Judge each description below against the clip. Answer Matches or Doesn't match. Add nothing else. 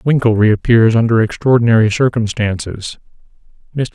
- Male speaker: Matches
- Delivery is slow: Matches